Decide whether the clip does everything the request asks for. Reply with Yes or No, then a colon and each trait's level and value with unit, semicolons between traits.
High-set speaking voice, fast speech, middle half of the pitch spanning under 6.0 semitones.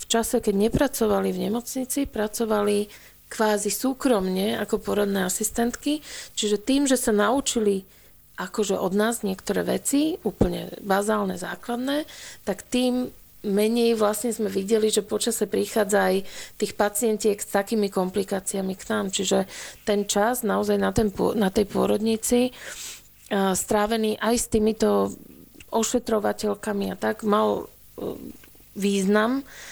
No: high, 210 Hz; average, 120 wpm; narrow, 2.4 semitones